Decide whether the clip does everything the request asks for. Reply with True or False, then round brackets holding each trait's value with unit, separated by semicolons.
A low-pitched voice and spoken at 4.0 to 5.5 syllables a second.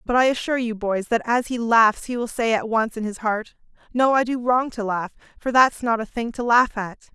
False (230 Hz; 5.3 syllables/s)